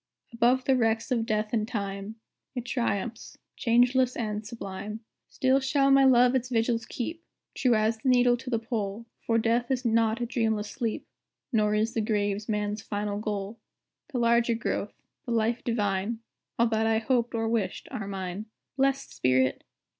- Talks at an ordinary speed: Yes, average, 170 wpm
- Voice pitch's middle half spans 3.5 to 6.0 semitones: No, narrow, 2.5 semitones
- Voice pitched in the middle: No, high, 230 Hz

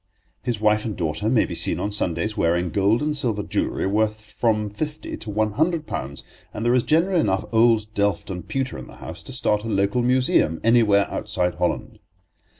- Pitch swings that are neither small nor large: Yes, average, 3.4 semitones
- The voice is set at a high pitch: No, low, 110 Hz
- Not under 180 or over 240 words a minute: Yes, average, 195 wpm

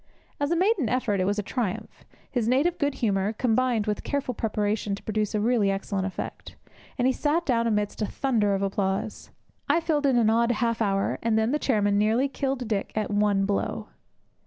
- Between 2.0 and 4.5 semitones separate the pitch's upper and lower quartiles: Yes, average, 3.9 semitones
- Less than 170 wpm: No, average, 200 wpm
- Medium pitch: No, high, 220 Hz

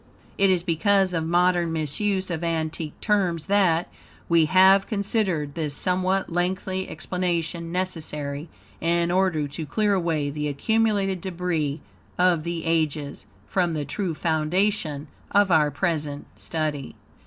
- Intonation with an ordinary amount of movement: Yes, average, 3.3 semitones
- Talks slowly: Yes, slow, 130 wpm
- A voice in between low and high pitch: Yes, medium, 170 Hz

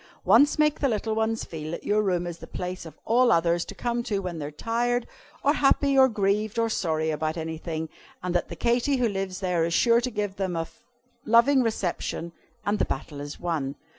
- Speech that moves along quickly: Yes, fast, 215 wpm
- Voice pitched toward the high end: Yes, high, 195 Hz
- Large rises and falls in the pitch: Yes, wide, 5.9 semitones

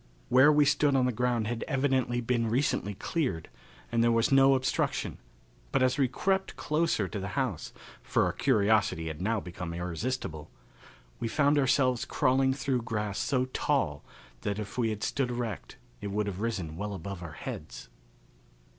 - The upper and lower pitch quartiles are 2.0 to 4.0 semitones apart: No, average, 4.7 semitones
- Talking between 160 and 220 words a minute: Yes, average, 165 wpm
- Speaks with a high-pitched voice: No, low, 115 Hz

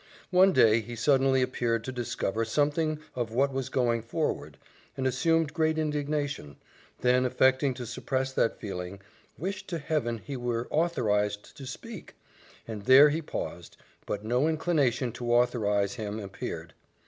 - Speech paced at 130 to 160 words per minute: Yes, average, 150 wpm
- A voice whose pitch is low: Yes, low, 130 Hz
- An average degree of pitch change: Yes, average, 4.6 semitones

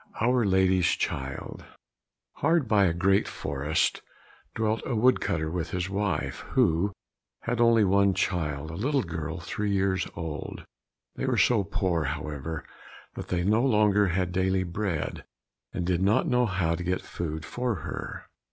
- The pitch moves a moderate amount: Yes, average, 4.2 semitones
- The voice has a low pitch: Yes, very low, 95 Hz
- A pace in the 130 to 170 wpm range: Yes, average, 160 wpm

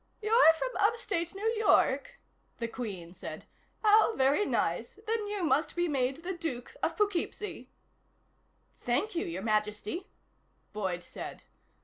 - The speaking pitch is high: Yes, very high, 335 Hz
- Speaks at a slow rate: Yes, slow, 130 wpm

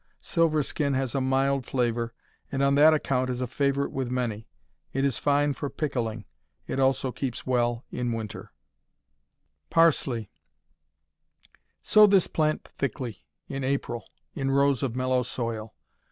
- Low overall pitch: Yes, low, 130 Hz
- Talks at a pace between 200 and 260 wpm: No, average, 140 wpm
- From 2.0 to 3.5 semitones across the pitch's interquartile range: Yes, narrow, 2.6 semitones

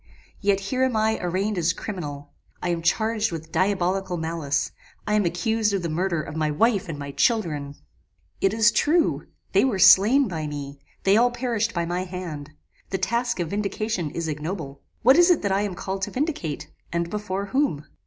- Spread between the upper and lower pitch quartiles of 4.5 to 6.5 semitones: Yes, average, 4.9 semitones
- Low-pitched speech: No, high, 190 Hz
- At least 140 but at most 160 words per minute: No, average, 190 wpm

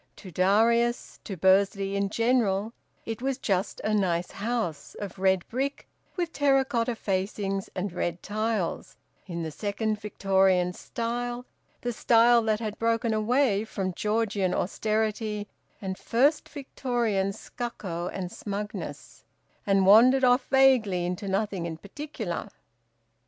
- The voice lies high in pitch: Yes, high, 210 Hz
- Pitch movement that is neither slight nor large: Yes, average, 3.6 semitones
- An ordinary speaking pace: No, slow, 130 wpm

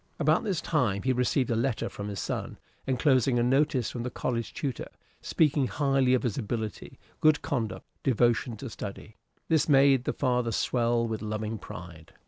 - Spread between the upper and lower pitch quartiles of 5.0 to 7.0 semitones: No, average, 3.4 semitones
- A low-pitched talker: Yes, low, 125 Hz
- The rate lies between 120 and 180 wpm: Yes, average, 170 wpm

